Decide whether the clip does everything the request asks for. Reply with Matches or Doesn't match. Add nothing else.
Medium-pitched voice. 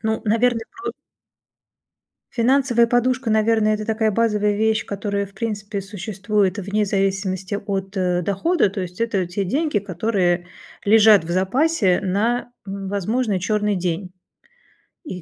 Doesn't match